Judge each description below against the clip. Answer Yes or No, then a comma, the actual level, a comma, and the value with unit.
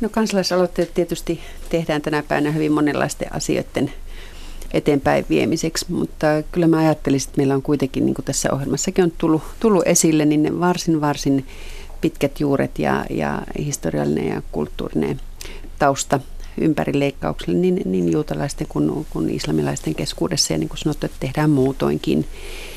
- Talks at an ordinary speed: Yes, average, 145 wpm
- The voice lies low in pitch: No, medium, 150 Hz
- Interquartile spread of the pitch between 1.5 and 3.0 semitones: No, average, 3.6 semitones